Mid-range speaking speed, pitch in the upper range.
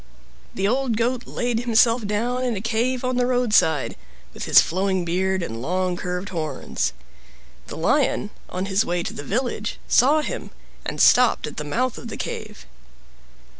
Yes: average, 170 wpm; high, 215 Hz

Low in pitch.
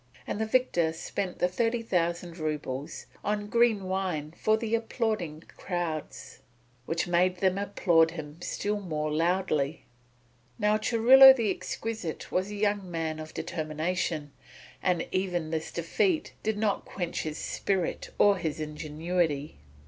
No: medium, 180 Hz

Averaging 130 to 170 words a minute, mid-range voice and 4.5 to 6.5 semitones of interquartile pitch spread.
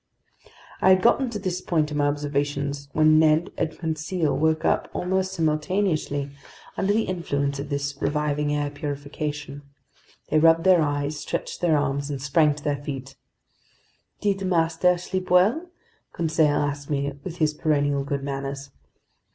No: average, 150 wpm; medium, 150 Hz; average, 3.2 semitones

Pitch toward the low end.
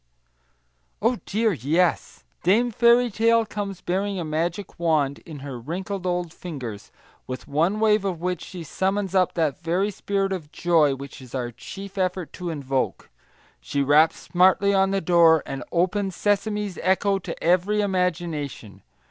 No: medium, 180 Hz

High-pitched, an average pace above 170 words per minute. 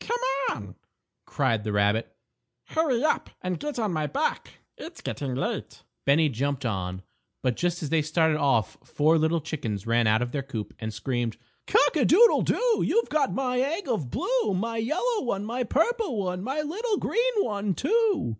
No: medium, 175 Hz; average, 180 wpm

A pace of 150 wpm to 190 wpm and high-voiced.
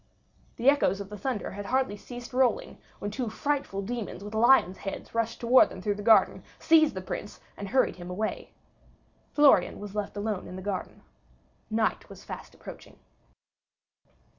Yes: average, 165 wpm; high, 215 Hz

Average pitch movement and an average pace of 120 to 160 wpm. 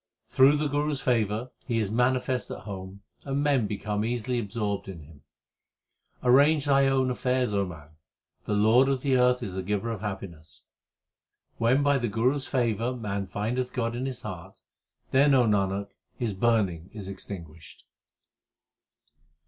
Yes: average, 4.4 semitones; average, 155 wpm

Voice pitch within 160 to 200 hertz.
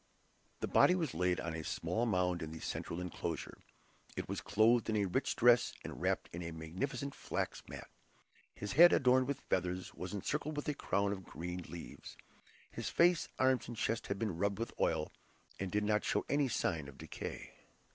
No: low, 100 Hz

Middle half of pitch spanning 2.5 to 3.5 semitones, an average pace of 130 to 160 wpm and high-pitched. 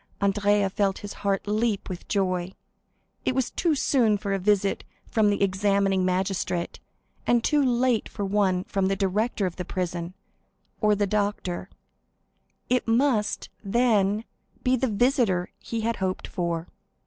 Yes: average, 3.2 semitones; average, 145 wpm; high, 200 Hz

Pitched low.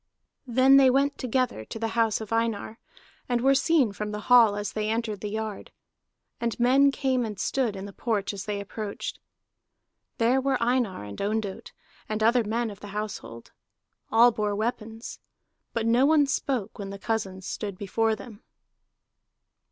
No: high, 225 Hz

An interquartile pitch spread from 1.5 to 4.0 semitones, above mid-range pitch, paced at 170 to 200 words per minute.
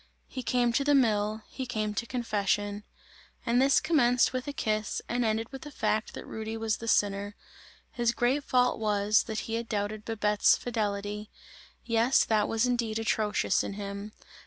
Yes: average, 2.7 semitones; high, 220 Hz; average, 175 wpm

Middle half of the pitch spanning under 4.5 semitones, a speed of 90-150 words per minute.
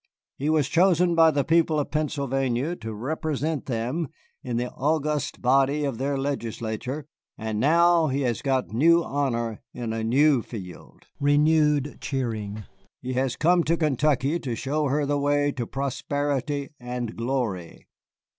Yes: average, 3.7 semitones; average, 145 wpm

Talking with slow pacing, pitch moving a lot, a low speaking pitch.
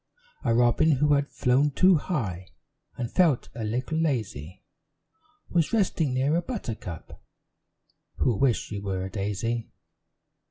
Yes: slow, 130 wpm; wide, 5.9 semitones; low, 125 Hz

